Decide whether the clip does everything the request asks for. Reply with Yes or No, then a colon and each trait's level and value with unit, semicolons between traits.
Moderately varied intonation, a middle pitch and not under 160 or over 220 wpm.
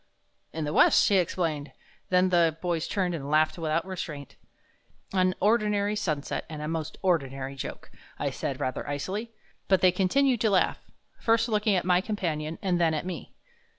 Yes: average, 4.2 semitones; medium, 180 Hz; average, 170 wpm